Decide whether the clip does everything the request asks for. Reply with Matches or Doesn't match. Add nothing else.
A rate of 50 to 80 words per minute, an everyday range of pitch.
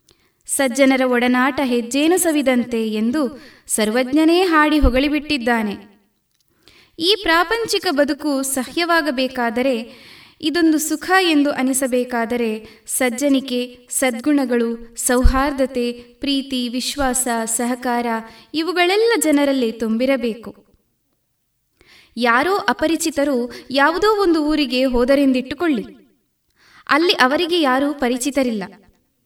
Matches